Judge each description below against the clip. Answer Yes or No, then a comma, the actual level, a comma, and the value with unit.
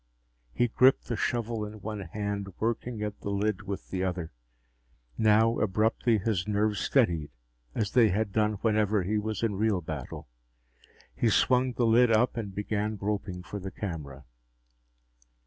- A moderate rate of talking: Yes, average, 155 wpm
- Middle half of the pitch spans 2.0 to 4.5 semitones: Yes, narrow, 2.4 semitones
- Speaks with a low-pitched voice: Yes, low, 105 Hz